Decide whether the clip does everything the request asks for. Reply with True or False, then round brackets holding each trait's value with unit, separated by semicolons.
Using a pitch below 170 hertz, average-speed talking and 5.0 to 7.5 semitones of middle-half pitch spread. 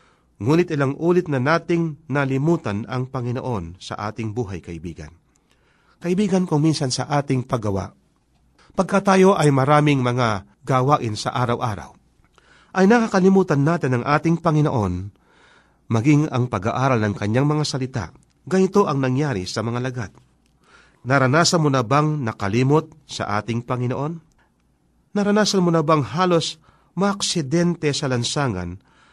True (135 Hz; 125 wpm; 5.6 semitones)